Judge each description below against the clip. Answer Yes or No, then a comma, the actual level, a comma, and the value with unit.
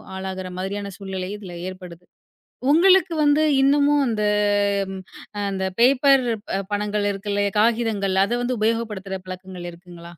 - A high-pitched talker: Yes, high, 205 Hz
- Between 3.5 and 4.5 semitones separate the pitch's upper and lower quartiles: Yes, average, 4.1 semitones